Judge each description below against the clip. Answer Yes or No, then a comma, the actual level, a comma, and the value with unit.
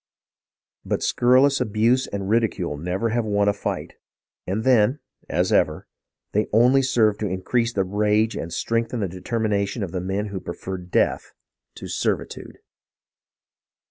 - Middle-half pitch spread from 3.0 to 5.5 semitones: Yes, average, 3.3 semitones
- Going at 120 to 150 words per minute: Yes, average, 145 wpm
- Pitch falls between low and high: No, low, 105 Hz